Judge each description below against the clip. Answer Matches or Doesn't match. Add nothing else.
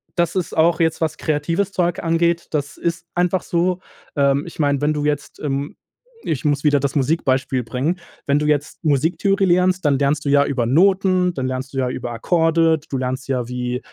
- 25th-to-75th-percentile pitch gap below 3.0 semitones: Doesn't match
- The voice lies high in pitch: Doesn't match